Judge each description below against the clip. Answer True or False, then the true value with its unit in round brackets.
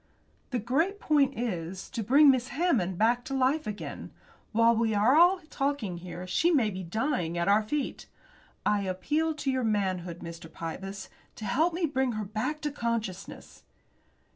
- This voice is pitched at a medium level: False (230 Hz)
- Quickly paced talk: False (165 wpm)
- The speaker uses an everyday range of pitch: False (6.7 semitones)